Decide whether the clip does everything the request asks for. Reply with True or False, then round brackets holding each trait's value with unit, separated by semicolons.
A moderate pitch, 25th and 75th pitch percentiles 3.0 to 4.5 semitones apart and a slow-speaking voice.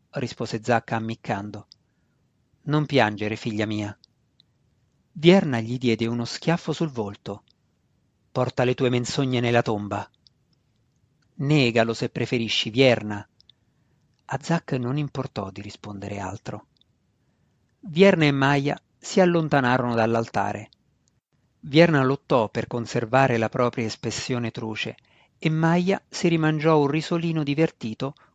False (125 Hz; 4.2 semitones; 110 wpm)